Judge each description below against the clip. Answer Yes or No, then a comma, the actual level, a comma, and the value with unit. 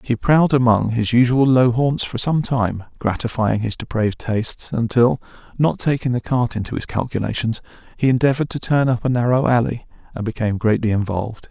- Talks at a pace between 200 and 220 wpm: No, average, 175 wpm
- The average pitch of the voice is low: Yes, low, 120 Hz